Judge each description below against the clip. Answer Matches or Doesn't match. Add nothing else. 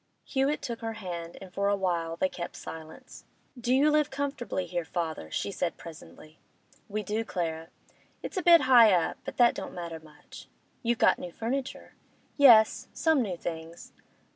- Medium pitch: Doesn't match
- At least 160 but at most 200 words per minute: Matches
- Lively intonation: Matches